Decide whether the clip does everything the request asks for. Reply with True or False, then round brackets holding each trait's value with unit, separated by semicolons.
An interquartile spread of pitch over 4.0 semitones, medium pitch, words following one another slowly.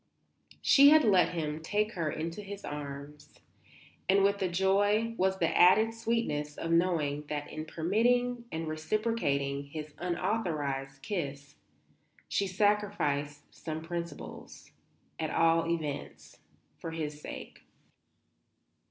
True (5.3 semitones; 165 Hz; 115 wpm)